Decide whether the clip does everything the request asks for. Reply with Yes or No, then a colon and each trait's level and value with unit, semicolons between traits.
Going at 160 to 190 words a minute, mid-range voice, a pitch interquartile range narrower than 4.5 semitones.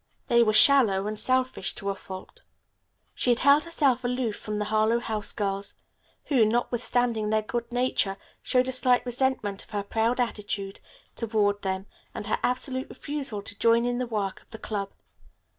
No: average, 175 wpm; high, 225 Hz; average, 3.3 semitones